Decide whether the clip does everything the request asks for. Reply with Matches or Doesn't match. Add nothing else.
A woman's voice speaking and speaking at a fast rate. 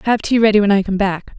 Matches